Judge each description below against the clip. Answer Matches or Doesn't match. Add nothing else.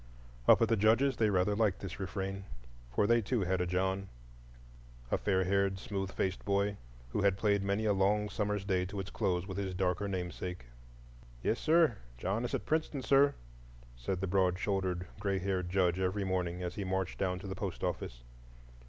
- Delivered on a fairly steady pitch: Matches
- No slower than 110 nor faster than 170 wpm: Doesn't match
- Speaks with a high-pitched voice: Doesn't match